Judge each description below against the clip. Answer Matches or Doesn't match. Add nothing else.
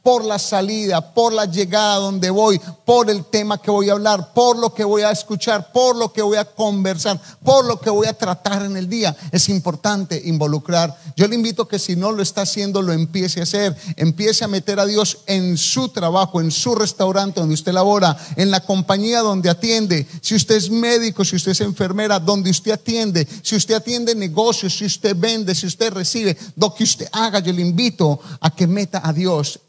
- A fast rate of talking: Matches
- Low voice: Doesn't match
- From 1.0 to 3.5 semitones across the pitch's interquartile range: Matches